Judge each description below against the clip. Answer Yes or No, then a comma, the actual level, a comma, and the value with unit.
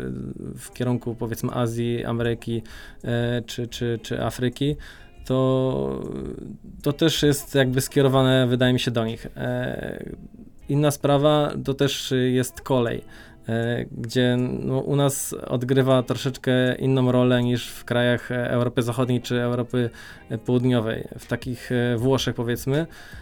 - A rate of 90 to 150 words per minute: Yes, average, 120 wpm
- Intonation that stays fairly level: Yes, narrow, 2.0 semitones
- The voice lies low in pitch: Yes, low, 125 Hz